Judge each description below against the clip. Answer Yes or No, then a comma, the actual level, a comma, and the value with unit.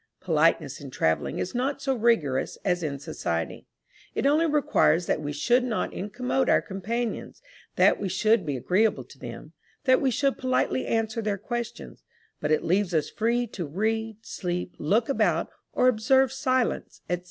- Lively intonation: Yes, wide, 6.3 semitones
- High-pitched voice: Yes, high, 220 Hz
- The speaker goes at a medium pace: Yes, average, 165 wpm